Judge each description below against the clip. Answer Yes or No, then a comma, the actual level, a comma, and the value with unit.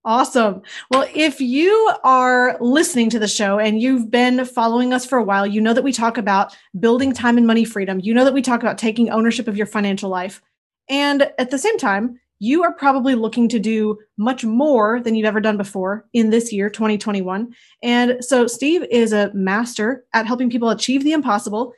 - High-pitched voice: Yes, high, 235 Hz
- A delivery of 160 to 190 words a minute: No, fast, 205 wpm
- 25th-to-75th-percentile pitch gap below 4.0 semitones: Yes, average, 3.0 semitones